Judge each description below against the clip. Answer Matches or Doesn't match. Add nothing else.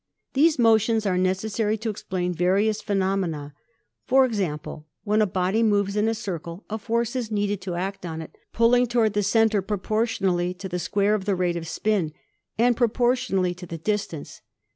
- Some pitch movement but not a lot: Matches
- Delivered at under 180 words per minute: Doesn't match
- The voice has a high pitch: Matches